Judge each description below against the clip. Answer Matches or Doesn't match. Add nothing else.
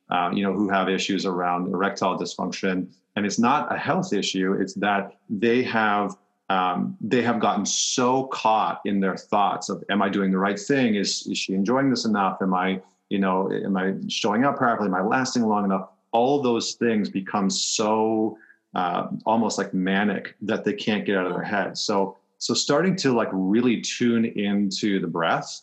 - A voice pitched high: Doesn't match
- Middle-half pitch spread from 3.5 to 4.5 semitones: Doesn't match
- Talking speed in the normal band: Matches